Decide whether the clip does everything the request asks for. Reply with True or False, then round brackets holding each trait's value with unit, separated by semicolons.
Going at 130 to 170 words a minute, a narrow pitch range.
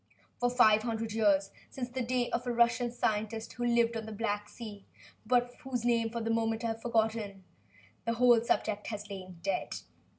False (190 wpm; 2.1 semitones)